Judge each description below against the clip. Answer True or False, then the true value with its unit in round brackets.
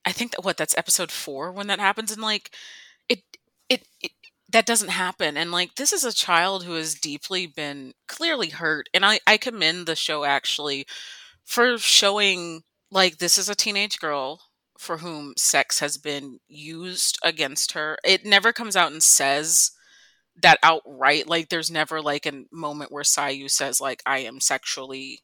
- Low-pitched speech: False (165 Hz)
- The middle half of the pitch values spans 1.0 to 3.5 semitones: False (5.3 semitones)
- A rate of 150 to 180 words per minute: True (175 wpm)